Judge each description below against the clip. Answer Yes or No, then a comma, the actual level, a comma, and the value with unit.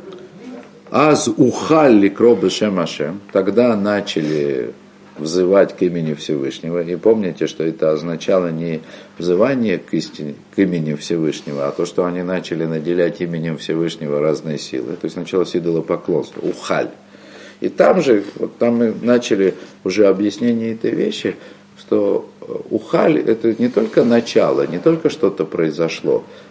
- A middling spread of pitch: No, wide, 5.8 semitones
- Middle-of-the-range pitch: No, very low, 90 Hz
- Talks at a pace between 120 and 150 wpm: Yes, average, 135 wpm